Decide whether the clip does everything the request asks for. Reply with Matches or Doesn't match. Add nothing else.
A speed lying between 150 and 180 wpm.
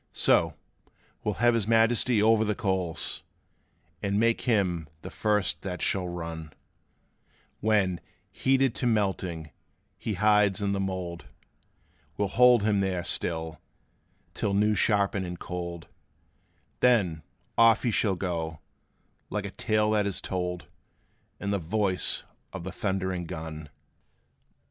Doesn't match